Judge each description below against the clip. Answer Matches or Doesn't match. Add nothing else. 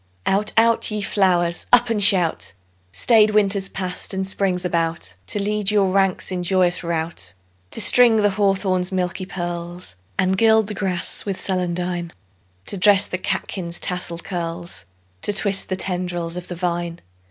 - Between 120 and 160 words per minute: Matches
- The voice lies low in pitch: Doesn't match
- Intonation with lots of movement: Doesn't match